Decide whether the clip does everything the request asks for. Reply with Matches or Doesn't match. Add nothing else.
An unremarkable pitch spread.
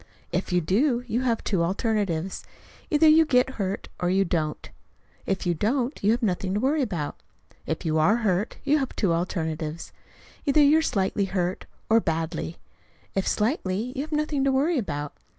Doesn't match